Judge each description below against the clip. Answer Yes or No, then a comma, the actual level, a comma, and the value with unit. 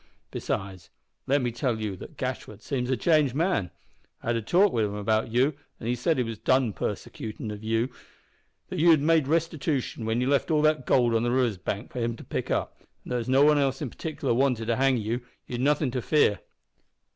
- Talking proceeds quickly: Yes, fast, 220 wpm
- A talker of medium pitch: No, low, 125 Hz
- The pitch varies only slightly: No, average, 4.2 semitones